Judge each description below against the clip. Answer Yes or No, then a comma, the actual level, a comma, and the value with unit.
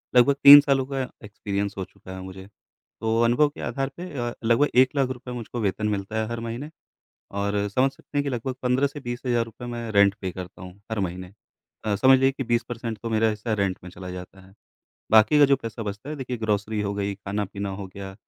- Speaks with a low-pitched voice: Yes, low, 110 Hz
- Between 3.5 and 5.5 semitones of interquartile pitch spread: Yes, average, 4.2 semitones